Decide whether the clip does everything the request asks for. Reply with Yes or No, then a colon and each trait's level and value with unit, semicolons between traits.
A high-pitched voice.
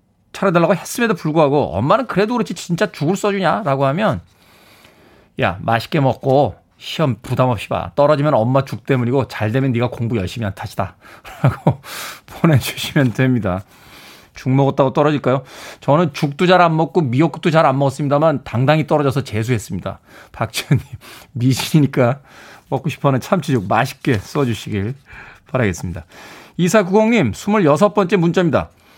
No: medium, 140 Hz